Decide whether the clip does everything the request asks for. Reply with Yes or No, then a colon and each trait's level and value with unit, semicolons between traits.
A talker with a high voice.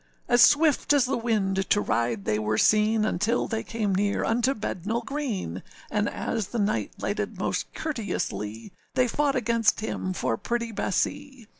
Yes: high, 220 Hz